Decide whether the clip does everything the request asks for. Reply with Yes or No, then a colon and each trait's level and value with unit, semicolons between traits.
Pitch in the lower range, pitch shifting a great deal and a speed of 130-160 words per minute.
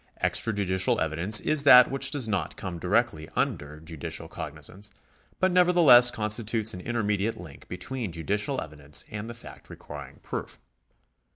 Yes: low, 105 Hz; wide, 6.2 semitones; slow, 135 wpm